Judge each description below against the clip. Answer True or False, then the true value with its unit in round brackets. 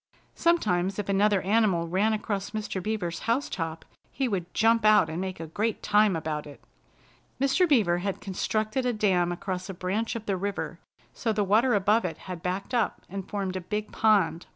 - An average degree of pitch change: True (3.2 semitones)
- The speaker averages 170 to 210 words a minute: True (190 wpm)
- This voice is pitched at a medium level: False (200 Hz)